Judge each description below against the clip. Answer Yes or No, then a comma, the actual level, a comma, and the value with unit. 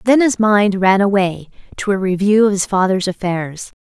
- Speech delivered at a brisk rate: No, average, 190 wpm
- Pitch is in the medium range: No, high, 195 Hz